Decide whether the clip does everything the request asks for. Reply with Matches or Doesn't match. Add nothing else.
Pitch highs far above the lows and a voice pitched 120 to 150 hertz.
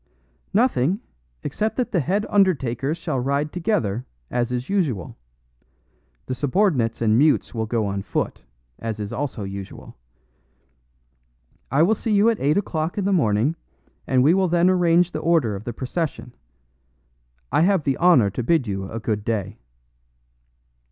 Matches